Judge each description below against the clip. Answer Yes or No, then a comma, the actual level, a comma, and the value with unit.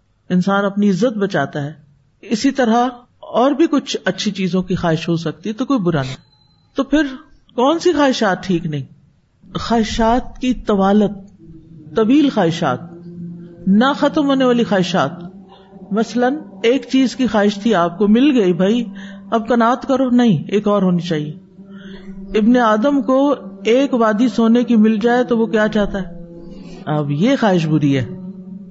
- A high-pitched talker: Yes, high, 205 Hz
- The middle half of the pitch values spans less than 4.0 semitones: No, wide, 5.5 semitones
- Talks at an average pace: Yes, average, 160 wpm